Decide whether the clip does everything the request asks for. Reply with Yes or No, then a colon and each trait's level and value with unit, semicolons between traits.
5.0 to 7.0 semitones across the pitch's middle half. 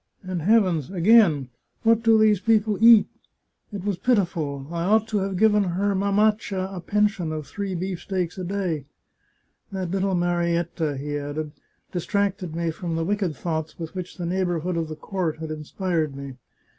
No: average, 3.8 semitones